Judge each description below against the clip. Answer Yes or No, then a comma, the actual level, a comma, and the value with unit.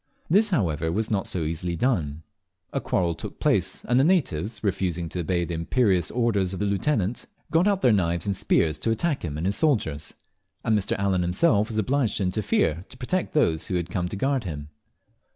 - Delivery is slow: No, fast, 205 wpm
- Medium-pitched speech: No, very low, 95 Hz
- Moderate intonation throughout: No, wide, 6.2 semitones